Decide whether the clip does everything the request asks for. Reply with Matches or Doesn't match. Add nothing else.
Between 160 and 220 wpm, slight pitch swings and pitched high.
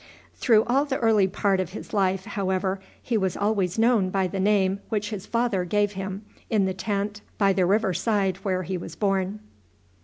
Matches